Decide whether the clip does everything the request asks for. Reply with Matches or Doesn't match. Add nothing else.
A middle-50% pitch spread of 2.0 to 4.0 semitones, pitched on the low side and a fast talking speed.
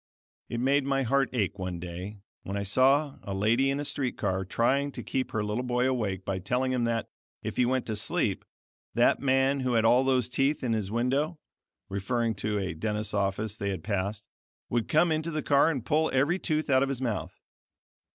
Doesn't match